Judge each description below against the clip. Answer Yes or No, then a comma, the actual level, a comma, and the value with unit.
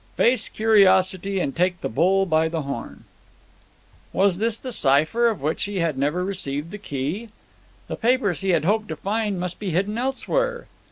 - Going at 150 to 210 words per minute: Yes, average, 175 wpm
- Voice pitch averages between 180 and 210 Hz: Yes, high, 190 Hz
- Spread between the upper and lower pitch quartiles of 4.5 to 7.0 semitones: Yes, average, 5.0 semitones